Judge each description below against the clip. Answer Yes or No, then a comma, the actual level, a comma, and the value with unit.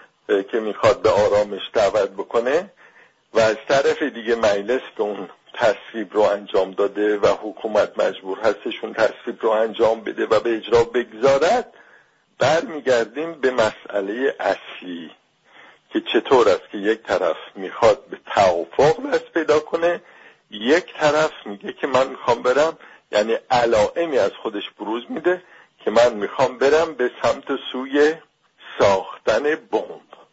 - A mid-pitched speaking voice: Yes, medium, 160 Hz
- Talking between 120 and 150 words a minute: Yes, slow, 135 wpm